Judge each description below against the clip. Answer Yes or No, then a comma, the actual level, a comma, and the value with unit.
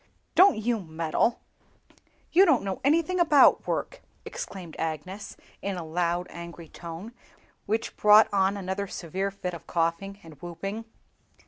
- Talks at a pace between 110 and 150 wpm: Yes, slow, 135 wpm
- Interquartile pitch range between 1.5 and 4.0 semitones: No, average, 4.4 semitones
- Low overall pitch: No, high, 190 Hz